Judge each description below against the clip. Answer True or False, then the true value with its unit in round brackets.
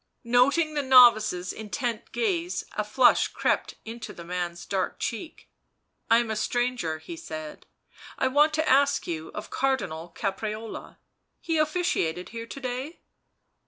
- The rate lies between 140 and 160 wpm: True (150 wpm)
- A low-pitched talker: False (235 Hz)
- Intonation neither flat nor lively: False (7.2 semitones)